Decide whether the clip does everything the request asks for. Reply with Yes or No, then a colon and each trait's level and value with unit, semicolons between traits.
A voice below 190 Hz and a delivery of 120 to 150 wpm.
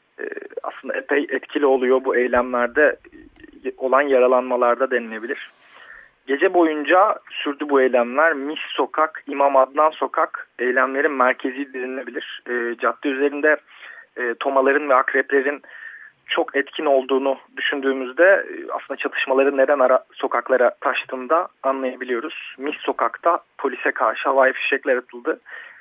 No: medium, 140 Hz; average, 105 wpm